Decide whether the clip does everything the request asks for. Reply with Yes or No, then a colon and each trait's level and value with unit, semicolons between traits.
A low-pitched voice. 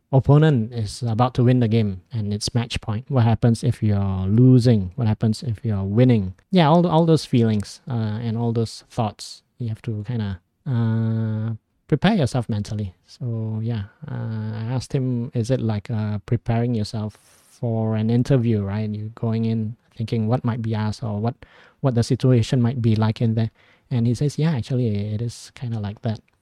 Yes: low, 115 Hz